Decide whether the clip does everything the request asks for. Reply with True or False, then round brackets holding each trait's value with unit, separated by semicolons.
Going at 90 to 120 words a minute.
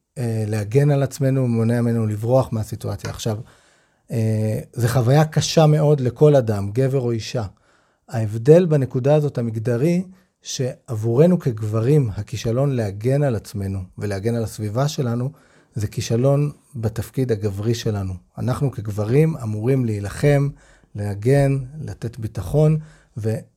True (110 wpm)